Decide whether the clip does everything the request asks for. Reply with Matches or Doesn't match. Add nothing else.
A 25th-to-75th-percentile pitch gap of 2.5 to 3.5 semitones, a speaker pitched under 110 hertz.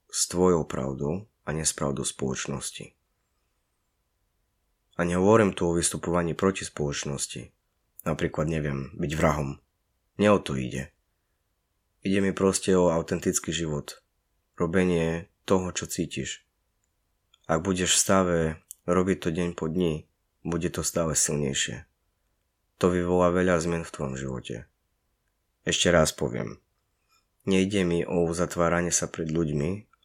Matches